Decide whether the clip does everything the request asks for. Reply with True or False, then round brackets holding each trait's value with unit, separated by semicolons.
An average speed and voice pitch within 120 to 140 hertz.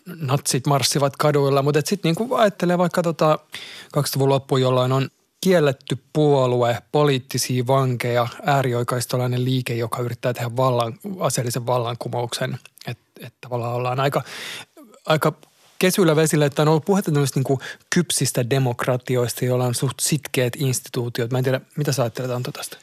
True (135 wpm; 135 Hz)